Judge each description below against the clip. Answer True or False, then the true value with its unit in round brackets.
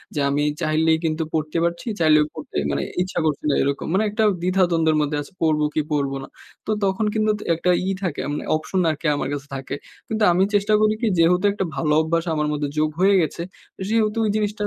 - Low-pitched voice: False (160 Hz)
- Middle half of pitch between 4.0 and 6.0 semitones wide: True (4.3 semitones)